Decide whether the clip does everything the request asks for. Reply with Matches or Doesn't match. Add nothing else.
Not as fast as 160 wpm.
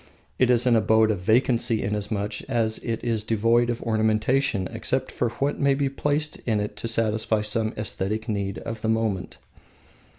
Doesn't match